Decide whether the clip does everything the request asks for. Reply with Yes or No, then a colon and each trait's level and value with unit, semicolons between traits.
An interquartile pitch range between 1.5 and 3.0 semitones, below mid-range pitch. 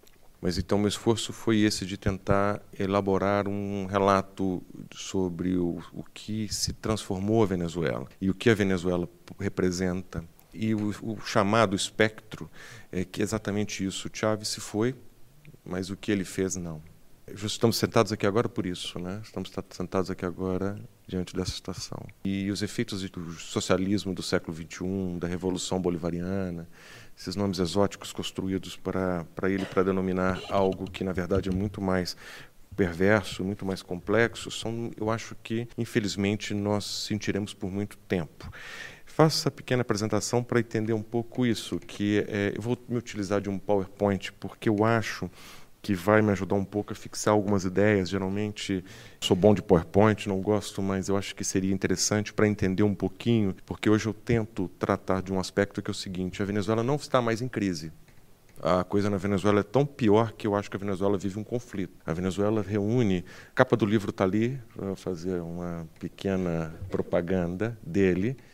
Yes: narrow, 2.5 semitones; low, 100 Hz